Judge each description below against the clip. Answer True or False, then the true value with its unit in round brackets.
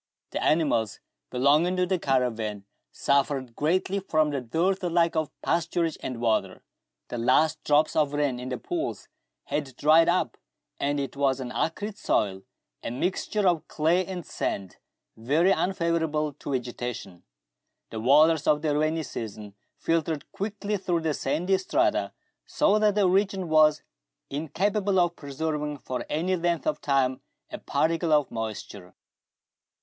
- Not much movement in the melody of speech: False (4.8 semitones)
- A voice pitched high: False (155 Hz)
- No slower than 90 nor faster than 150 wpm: True (145 wpm)